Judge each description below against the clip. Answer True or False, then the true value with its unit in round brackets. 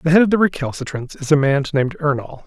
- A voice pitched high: False (150 Hz)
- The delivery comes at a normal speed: False (245 wpm)